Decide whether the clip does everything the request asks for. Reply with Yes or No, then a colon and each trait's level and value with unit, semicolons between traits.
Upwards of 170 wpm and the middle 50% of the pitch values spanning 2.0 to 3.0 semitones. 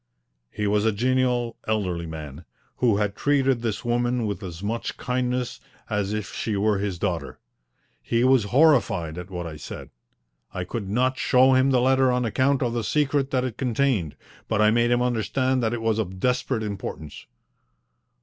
No: average, 180 wpm; average, 4.0 semitones